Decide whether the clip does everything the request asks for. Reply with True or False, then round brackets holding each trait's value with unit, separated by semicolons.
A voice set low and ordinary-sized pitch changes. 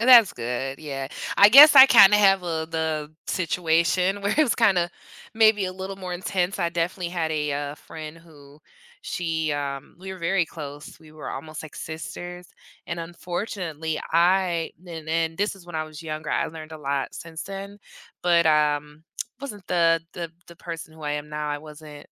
False (165 Hz; 3.2 semitones)